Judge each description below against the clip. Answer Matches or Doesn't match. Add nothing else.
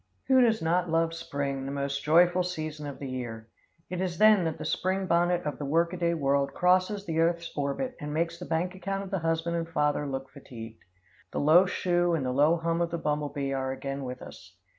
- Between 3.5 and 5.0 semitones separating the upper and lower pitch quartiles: Matches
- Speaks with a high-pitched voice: Doesn't match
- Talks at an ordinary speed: Doesn't match